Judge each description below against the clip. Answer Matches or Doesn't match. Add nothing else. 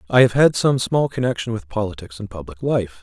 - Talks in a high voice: Doesn't match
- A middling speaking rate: Doesn't match